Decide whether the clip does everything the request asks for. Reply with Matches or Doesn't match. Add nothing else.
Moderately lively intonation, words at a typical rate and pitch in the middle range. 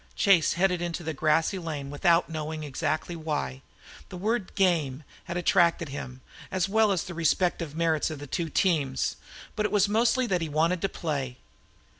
Matches